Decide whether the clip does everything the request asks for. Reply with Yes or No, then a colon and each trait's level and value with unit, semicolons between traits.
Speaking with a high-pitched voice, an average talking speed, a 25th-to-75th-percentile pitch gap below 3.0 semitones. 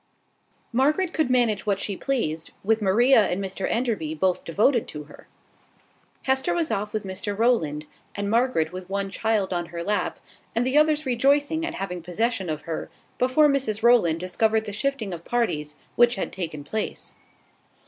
No: high, 215 Hz; average, 170 wpm; wide, 5.5 semitones